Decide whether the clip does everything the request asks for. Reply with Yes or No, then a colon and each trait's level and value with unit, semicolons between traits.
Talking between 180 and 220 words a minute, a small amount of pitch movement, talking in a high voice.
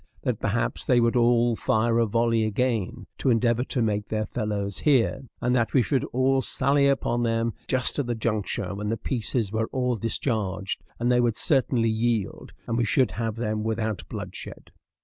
No: average, 185 wpm; narrow, 2.3 semitones; low, 115 Hz